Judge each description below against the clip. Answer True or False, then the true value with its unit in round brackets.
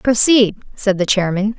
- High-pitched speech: True (210 Hz)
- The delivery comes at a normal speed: True (150 wpm)